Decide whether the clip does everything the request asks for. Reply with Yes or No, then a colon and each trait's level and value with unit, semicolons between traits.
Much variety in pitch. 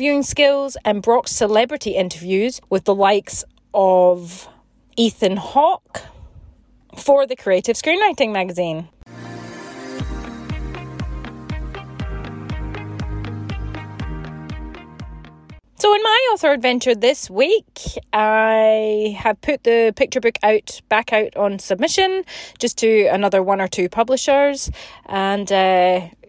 Yes: wide, 6.3 semitones